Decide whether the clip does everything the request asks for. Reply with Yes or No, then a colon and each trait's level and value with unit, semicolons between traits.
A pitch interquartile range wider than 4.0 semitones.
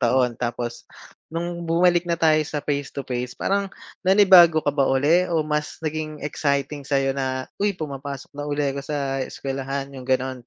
No: average, 3.4 semitones